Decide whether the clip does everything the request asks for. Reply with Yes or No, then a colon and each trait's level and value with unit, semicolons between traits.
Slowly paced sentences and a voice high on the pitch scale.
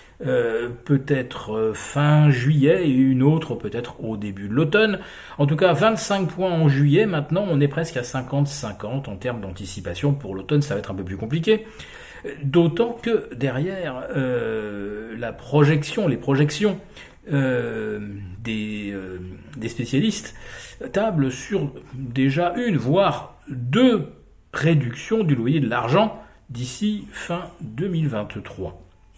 No: slow, 130 wpm; medium, 140 Hz